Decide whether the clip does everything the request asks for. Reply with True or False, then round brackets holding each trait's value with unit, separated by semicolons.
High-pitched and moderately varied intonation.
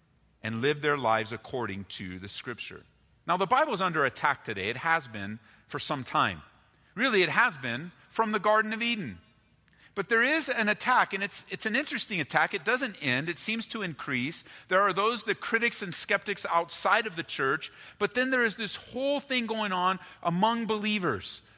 False (195 Hz; 7.8 semitones)